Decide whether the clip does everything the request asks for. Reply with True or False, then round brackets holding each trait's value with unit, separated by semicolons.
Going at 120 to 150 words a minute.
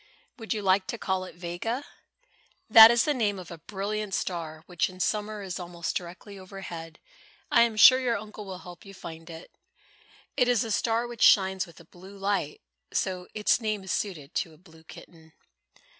False (190 wpm)